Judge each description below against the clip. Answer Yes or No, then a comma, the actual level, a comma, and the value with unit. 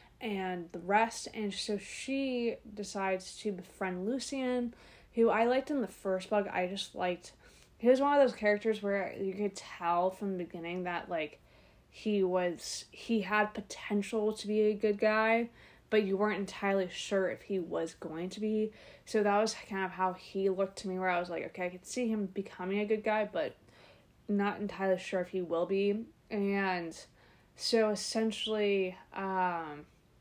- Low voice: No, high, 200 Hz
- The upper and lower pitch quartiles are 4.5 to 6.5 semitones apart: No, narrow, 2.6 semitones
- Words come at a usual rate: Yes, average, 180 wpm